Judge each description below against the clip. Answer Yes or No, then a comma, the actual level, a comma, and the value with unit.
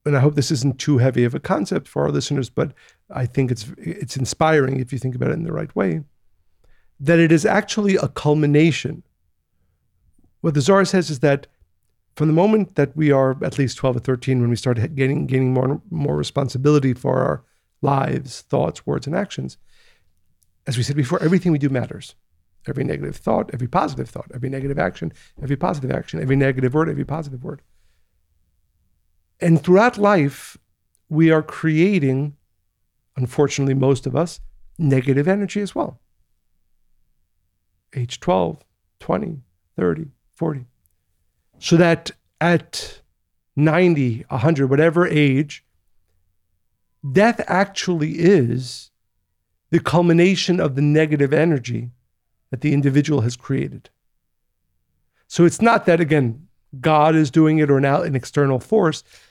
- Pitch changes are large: Yes, wide, 7.7 semitones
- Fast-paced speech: No, average, 150 wpm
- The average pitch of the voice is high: No, low, 135 Hz